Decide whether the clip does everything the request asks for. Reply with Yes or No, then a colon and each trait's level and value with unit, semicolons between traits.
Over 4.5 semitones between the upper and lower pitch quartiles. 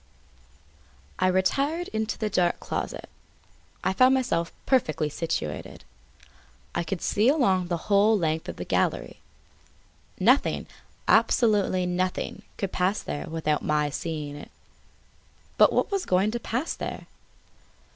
Yes: average, 5.0 semitones